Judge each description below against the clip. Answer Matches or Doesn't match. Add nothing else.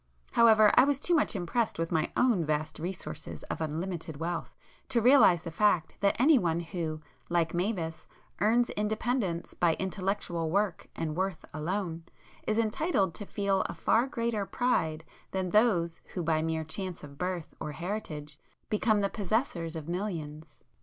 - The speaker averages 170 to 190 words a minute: Doesn't match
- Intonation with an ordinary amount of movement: Matches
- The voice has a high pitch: Doesn't match